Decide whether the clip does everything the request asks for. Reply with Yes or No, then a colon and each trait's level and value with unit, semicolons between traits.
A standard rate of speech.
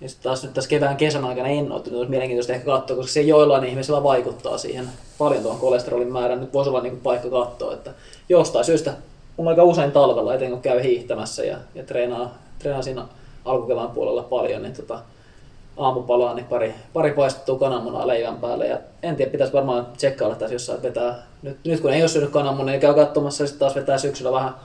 No: fast, 195 wpm